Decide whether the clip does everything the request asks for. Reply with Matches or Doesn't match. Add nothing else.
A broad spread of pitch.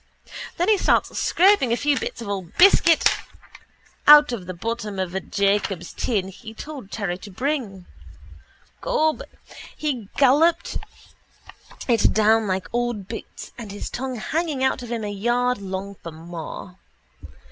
Matches